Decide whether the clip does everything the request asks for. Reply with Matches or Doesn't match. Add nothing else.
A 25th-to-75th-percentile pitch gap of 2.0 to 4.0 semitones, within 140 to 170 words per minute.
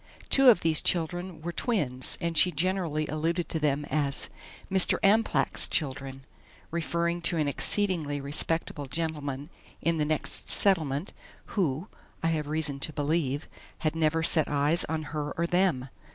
Matches